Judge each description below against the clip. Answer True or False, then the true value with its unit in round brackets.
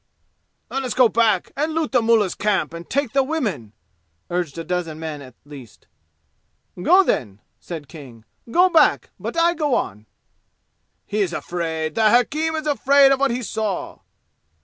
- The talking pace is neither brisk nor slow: True (165 wpm)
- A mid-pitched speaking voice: False (215 Hz)